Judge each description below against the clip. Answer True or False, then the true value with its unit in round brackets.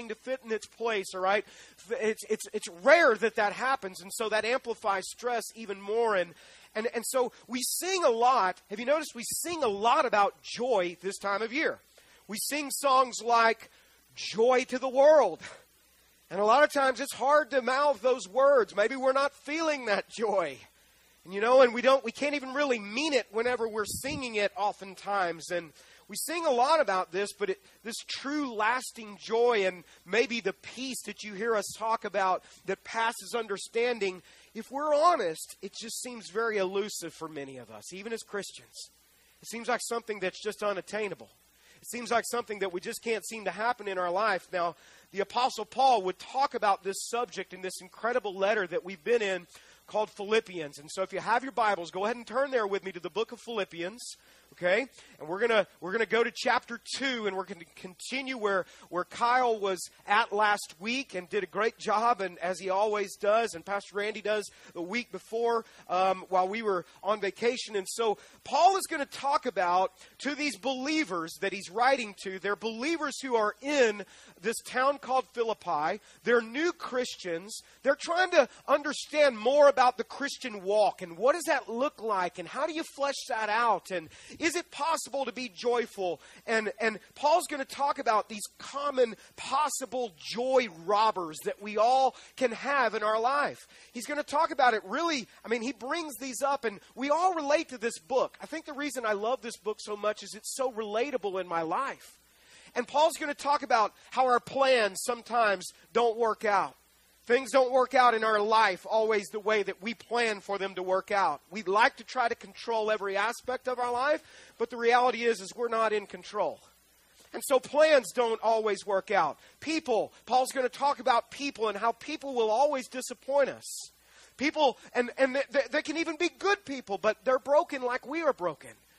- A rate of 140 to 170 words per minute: False (200 wpm)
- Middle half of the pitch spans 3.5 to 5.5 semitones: True (4.7 semitones)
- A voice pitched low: False (230 Hz)